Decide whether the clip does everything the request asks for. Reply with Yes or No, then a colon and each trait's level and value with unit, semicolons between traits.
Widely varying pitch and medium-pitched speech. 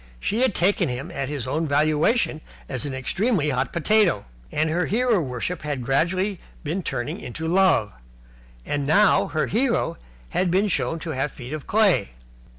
Yes: wide, 5.8 semitones; medium, 160 Hz